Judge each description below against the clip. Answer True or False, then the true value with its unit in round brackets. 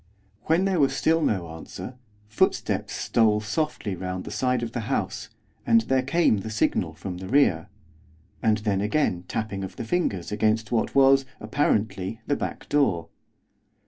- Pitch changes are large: True (5.8 semitones)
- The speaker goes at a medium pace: True (155 wpm)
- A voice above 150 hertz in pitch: False (110 Hz)